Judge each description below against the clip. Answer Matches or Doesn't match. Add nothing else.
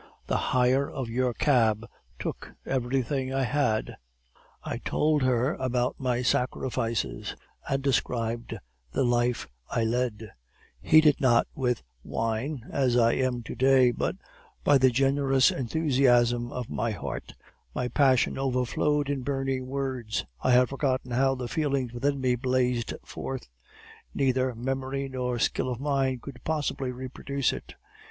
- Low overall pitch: Matches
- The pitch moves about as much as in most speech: Doesn't match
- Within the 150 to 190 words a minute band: Doesn't match